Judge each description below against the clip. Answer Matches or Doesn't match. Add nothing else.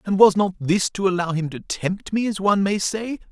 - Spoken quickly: Matches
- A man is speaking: Matches